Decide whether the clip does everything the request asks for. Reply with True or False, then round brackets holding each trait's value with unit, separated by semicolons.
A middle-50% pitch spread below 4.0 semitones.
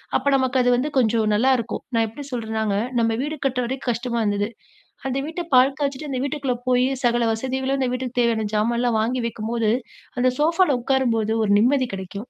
True (2.9 semitones)